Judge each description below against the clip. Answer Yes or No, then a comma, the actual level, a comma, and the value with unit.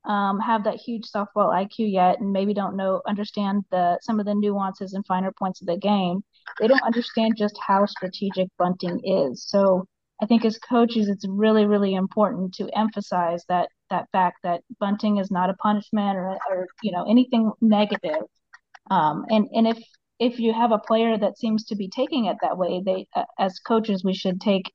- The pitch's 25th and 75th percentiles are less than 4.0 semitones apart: Yes, average, 2.8 semitones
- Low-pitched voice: No, high, 205 Hz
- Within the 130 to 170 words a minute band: No, average, 195 wpm